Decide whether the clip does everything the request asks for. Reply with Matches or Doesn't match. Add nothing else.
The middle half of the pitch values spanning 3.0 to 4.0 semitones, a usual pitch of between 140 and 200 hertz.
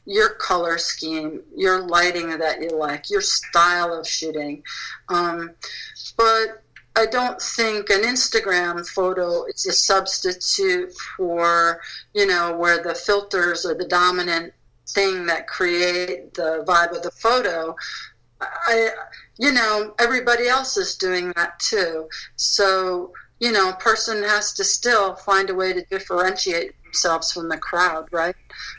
Doesn't match